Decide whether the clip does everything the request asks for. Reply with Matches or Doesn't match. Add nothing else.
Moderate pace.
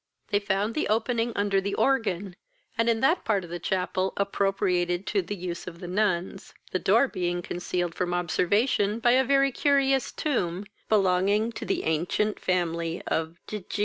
Matches